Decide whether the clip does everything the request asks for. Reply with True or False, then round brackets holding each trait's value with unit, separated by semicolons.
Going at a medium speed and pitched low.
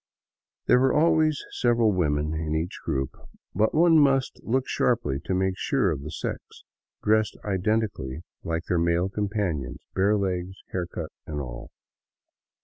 True (145 wpm; 95 Hz)